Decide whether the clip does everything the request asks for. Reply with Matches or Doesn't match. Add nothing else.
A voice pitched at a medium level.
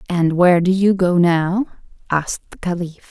Matches